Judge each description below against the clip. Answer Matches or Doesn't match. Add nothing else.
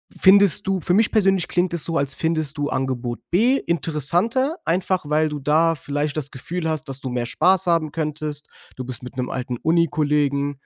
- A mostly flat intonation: Doesn't match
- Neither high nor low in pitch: Matches